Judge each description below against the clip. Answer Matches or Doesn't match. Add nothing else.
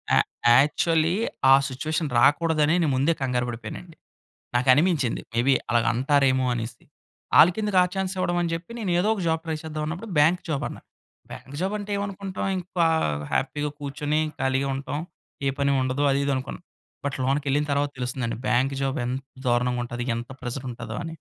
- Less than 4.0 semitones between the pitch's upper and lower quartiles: Doesn't match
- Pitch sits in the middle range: Matches